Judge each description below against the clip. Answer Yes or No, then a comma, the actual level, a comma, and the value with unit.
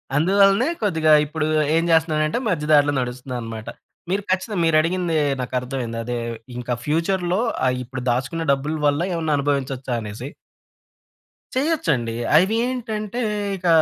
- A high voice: No, medium, 155 Hz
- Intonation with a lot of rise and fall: Yes, wide, 6.3 semitones